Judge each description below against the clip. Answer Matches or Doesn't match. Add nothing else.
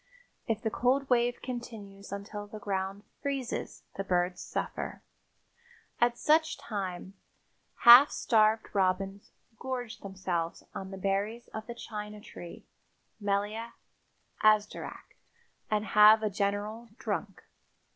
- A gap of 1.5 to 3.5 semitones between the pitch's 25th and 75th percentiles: Matches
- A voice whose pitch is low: Doesn't match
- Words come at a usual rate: Doesn't match